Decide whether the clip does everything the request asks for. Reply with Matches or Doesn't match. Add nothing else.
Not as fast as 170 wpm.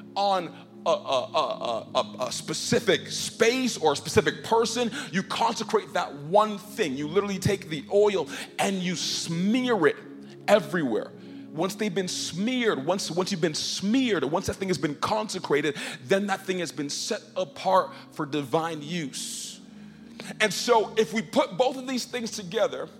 Matches